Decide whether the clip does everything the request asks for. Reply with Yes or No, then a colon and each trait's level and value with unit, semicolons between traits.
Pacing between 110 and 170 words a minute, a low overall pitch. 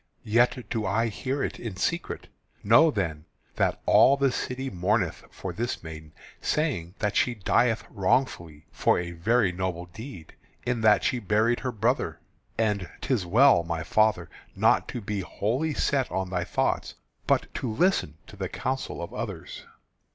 Yes: average, 160 wpm; low, 105 Hz